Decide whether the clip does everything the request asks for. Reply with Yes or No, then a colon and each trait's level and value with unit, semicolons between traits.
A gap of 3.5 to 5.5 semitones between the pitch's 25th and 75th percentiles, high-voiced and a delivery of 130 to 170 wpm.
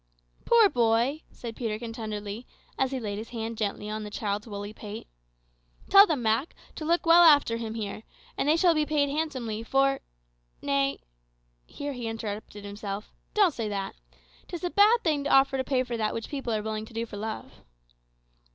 No: average, 5.1 semitones; high, 230 Hz; average, 190 wpm